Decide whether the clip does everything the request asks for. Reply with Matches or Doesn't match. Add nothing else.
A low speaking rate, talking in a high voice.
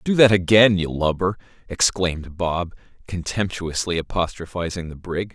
Doesn't match